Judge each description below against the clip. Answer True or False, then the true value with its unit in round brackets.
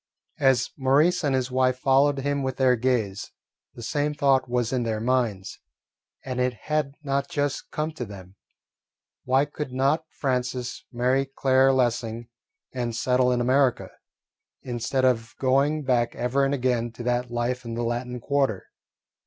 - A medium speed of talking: True (155 wpm)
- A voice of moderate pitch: False (130 Hz)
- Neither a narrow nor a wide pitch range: False (2.2 semitones)